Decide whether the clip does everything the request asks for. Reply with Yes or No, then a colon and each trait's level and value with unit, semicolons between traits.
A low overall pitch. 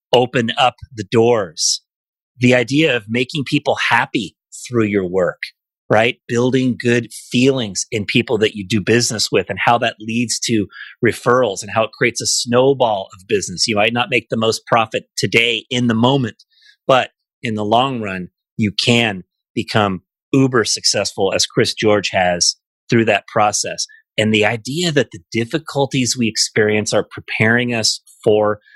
Yes: low, 120 Hz